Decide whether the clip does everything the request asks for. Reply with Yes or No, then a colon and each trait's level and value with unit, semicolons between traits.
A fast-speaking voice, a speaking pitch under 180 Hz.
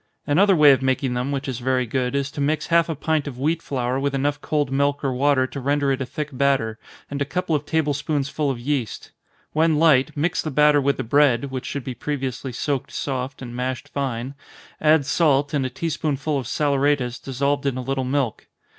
Yes: fast, 215 wpm; medium, 140 Hz